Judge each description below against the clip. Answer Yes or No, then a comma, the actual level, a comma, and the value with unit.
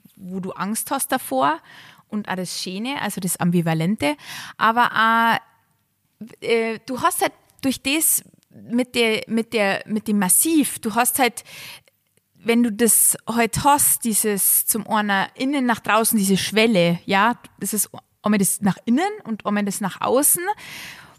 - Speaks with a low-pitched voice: No, high, 220 Hz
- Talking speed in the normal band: Yes, average, 160 wpm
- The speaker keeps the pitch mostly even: No, average, 3.9 semitones